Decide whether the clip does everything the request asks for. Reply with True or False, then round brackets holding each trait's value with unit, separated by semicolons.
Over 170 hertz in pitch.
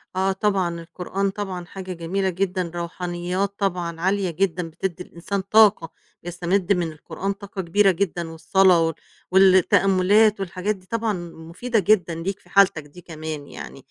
True (185 Hz)